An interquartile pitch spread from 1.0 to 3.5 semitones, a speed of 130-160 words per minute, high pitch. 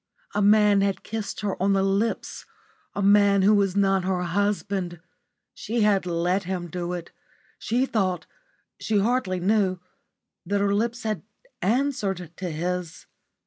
Yes: narrow, 2.5 semitones; average, 145 wpm; high, 195 Hz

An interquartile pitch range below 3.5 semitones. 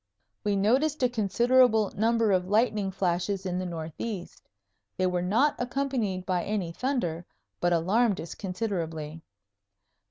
No: average, 4.6 semitones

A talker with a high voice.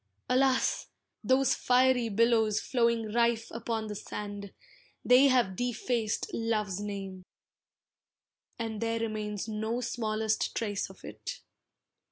Yes: high, 225 Hz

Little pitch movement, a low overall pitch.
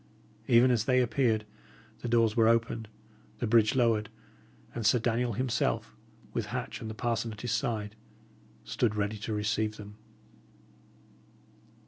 Yes: narrow, 1.8 semitones; low, 115 Hz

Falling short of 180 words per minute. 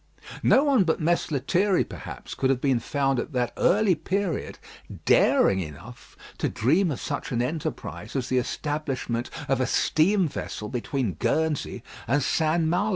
Yes: average, 160 wpm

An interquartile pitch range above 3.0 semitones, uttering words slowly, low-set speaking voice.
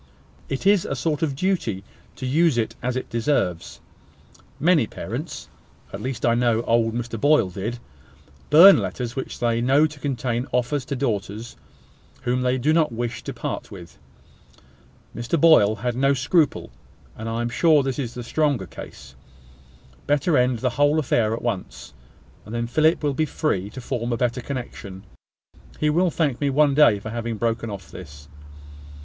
No: average, 4.1 semitones; average, 170 wpm; low, 125 Hz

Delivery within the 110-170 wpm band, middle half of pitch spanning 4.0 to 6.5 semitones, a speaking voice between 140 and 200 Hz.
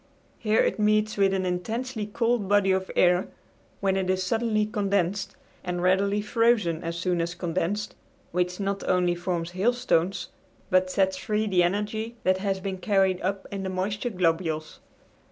No: average, 160 wpm; narrow, 2.6 semitones; high, 190 Hz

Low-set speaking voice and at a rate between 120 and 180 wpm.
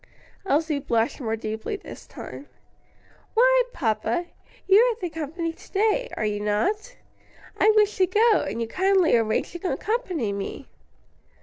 No: very high, 340 Hz; average, 145 wpm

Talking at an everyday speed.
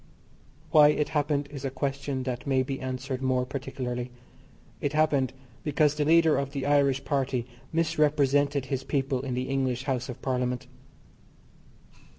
Yes: average, 150 wpm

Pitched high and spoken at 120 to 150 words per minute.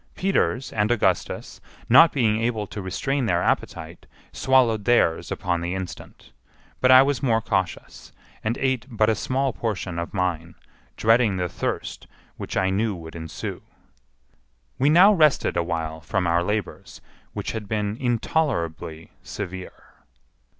No: low, 105 Hz; average, 145 wpm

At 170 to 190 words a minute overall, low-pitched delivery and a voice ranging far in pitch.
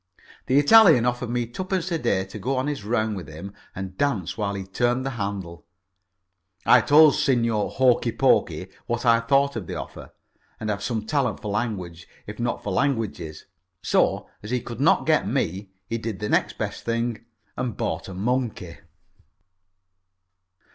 No: average, 175 wpm; low, 115 Hz; average, 4.3 semitones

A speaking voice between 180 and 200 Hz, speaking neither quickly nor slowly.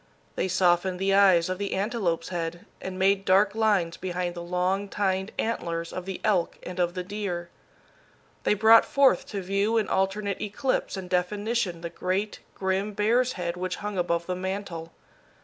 Yes: high, 190 Hz; average, 170 wpm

